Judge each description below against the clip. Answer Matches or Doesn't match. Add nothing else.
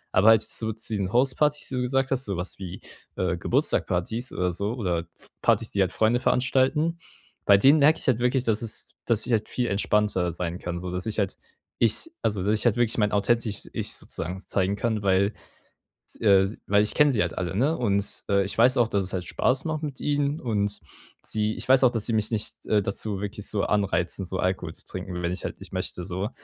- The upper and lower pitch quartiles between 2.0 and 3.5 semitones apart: Doesn't match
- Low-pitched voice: Matches